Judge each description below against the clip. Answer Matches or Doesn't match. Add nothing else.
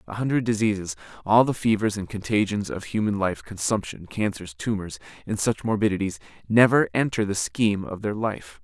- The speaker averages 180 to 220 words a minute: Doesn't match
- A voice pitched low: Matches